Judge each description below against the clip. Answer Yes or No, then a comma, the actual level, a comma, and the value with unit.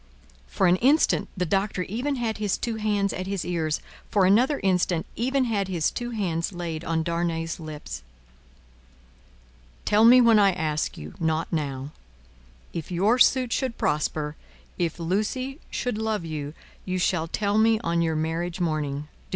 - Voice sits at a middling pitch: Yes, medium, 180 Hz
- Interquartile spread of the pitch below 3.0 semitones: No, average, 5.1 semitones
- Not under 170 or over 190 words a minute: No, average, 160 wpm